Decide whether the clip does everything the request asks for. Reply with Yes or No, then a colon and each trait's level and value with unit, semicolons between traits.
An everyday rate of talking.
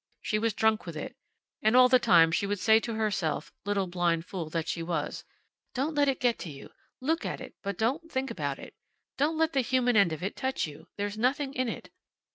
No: fast, 225 wpm